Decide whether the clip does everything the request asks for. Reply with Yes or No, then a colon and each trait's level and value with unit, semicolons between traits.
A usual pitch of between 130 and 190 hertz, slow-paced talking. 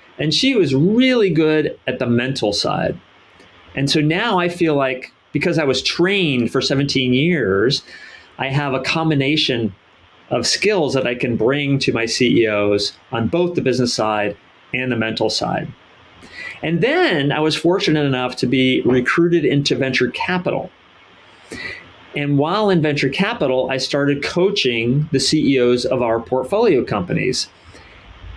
No: low, 135 Hz; average, 150 wpm